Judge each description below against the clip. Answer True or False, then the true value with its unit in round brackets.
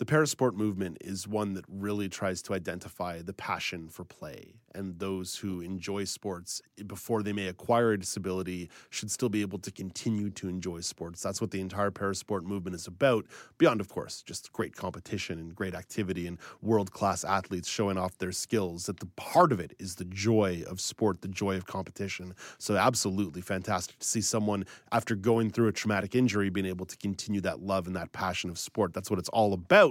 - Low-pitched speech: True (100 Hz)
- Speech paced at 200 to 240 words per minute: True (205 wpm)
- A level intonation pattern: True (2.2 semitones)